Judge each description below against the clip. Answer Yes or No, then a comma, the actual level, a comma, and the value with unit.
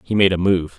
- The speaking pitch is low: Yes, very low, 95 Hz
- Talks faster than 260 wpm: Yes, fast, 305 wpm